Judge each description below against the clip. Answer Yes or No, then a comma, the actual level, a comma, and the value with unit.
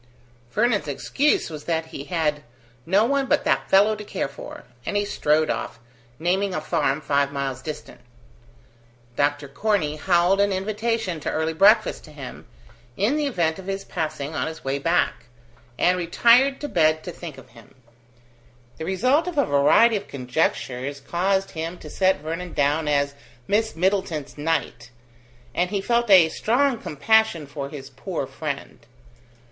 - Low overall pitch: No, medium, 170 Hz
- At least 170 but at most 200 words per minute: No, average, 160 wpm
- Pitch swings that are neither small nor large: No, wide, 5.7 semitones